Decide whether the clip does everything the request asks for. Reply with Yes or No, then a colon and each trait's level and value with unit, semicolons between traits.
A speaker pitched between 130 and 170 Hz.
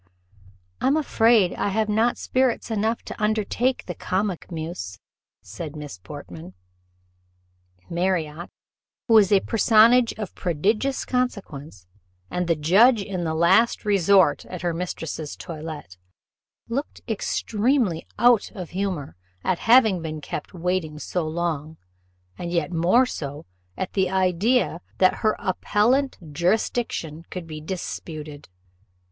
No: medium, 185 Hz